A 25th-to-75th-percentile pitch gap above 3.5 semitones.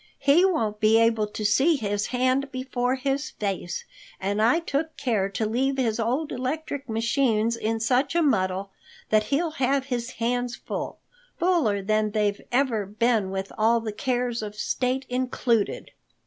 Yes: average, 4.0 semitones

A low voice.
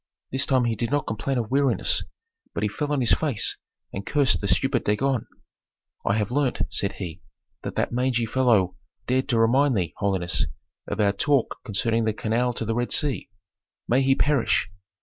Yes: low, 120 Hz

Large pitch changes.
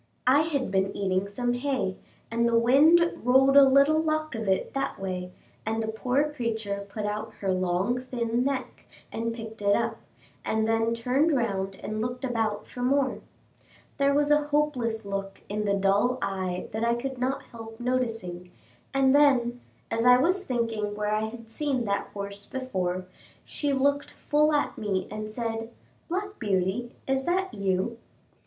No: average, 4.6 semitones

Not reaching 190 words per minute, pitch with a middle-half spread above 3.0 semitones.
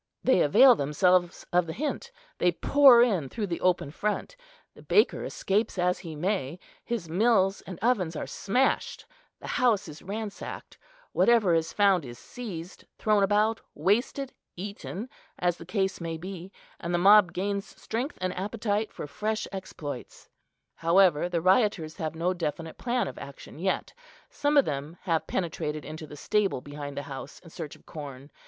Yes: average, 165 wpm; average, 4.7 semitones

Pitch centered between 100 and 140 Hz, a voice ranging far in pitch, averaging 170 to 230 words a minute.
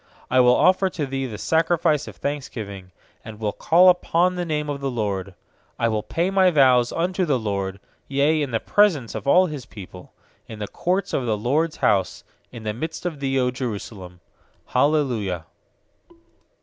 Yes: low, 135 Hz; wide, 7.0 semitones; average, 175 wpm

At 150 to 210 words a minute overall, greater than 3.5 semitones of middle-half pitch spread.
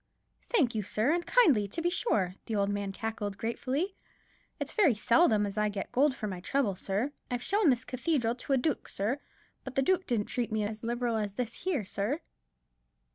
Yes: average, 200 wpm; wide, 5.5 semitones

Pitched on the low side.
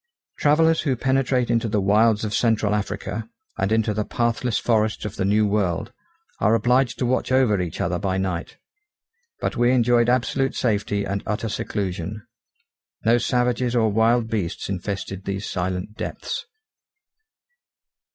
Yes: low, 110 Hz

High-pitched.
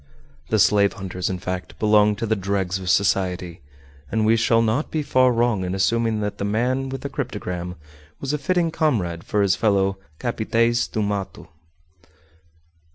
No: low, 105 Hz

